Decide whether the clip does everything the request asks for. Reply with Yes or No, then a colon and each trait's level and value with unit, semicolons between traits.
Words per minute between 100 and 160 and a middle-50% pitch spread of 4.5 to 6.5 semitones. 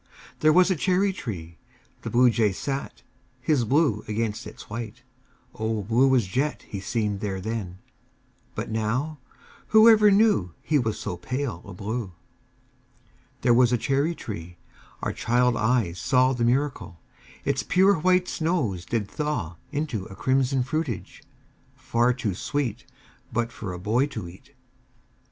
Yes: average, 145 wpm; wide, 5.5 semitones